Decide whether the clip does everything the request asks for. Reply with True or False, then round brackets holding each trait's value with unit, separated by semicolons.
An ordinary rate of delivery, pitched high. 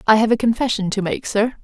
False (255 wpm; 220 Hz)